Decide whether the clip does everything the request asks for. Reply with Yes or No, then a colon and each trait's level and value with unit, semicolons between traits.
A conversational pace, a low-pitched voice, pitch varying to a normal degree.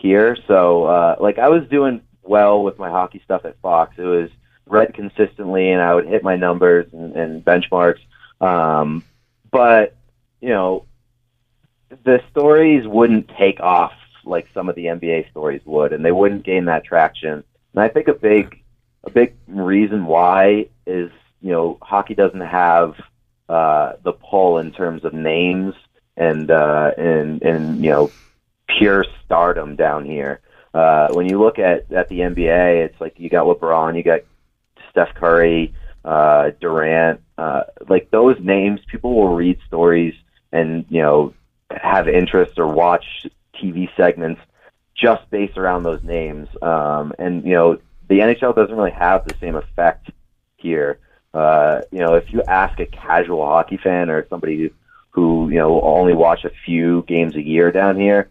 Yes: average, 165 wpm; very low, 90 Hz; average, 3.9 semitones